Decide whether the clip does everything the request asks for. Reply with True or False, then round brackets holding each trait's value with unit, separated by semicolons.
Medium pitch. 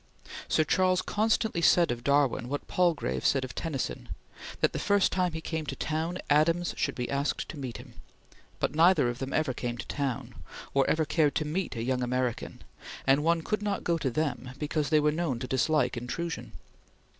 True (150 Hz)